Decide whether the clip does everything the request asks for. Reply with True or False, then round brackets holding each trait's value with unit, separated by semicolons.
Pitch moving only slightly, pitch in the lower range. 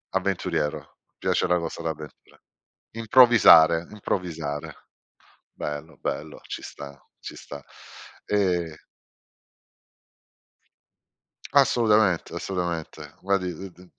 False (3.8 semitones; 85 Hz)